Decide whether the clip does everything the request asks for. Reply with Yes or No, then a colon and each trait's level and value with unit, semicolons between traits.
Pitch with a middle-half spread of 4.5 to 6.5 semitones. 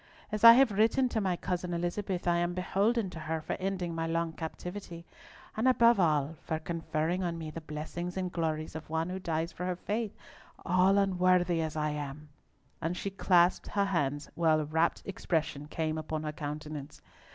No: average, 3.0 semitones